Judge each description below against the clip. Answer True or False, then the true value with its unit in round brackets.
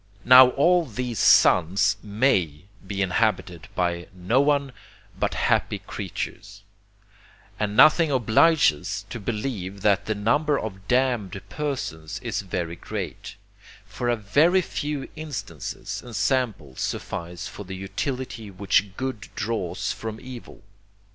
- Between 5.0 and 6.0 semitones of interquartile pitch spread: True (5.5 semitones)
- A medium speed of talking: False (120 wpm)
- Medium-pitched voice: False (110 Hz)